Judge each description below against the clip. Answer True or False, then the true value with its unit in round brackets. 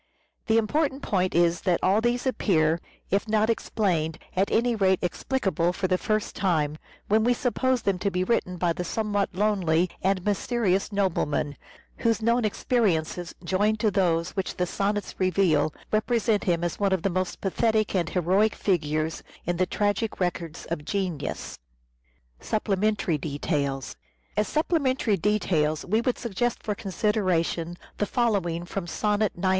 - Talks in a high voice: True (195 Hz)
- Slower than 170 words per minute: True (150 wpm)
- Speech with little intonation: False (3.8 semitones)